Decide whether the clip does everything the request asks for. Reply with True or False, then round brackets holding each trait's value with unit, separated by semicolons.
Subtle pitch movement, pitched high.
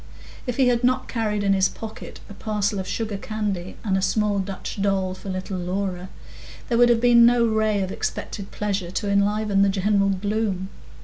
True (2.2 semitones; 205 Hz)